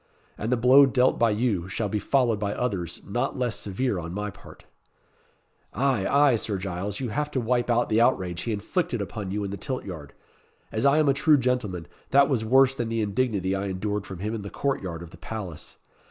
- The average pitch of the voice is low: Yes, low, 110 Hz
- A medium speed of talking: No, fast, 220 wpm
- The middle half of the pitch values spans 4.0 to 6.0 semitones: Yes, average, 4.6 semitones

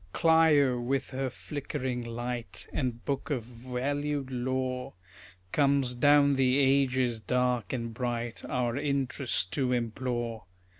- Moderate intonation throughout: No, narrow, 2.3 semitones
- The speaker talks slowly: Yes, slow, 115 wpm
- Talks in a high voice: No, low, 130 Hz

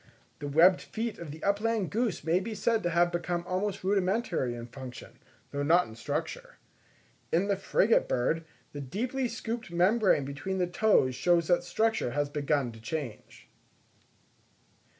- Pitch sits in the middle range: Yes, medium, 175 Hz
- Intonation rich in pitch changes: Yes, wide, 6.2 semitones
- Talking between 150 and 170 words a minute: Yes, average, 155 wpm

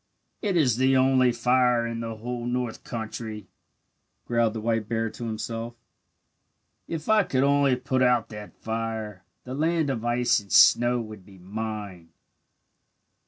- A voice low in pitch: Yes, low, 115 Hz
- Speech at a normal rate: Yes, average, 150 wpm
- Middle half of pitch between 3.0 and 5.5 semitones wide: No, narrow, 2.5 semitones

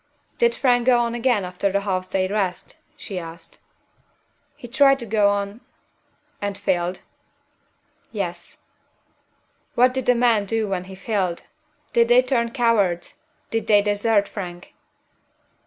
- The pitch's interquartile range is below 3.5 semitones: No, average, 4.1 semitones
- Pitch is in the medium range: No, high, 205 Hz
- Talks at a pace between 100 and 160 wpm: Yes, average, 140 wpm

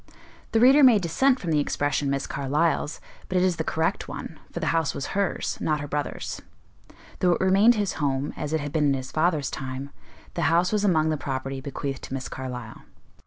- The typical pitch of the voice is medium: Yes, medium, 155 Hz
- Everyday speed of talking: No, fast, 210 wpm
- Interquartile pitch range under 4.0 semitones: No, average, 4.6 semitones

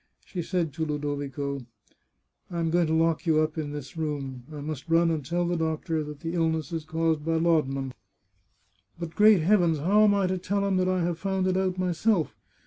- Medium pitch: Yes, medium, 165 Hz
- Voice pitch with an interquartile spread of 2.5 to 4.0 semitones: Yes, average, 2.9 semitones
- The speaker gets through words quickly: Yes, fast, 215 wpm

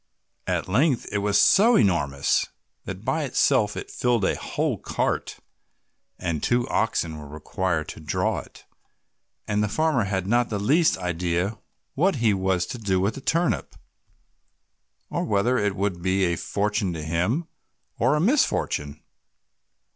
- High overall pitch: No, low, 100 Hz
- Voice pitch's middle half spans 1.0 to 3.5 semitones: No, wide, 5.5 semitones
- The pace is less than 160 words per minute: Yes, average, 150 wpm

